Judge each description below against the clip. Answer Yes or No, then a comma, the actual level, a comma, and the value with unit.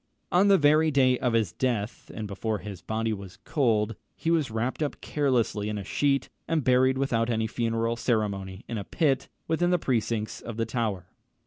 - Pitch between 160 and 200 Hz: No, low, 115 Hz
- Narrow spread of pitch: No, average, 4.2 semitones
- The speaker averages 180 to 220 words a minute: Yes, average, 190 wpm